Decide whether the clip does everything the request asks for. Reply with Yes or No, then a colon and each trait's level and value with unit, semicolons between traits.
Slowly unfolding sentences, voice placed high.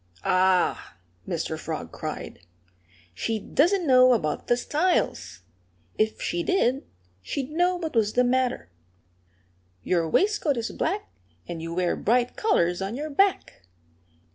Yes: slow, 130 wpm; high, 245 Hz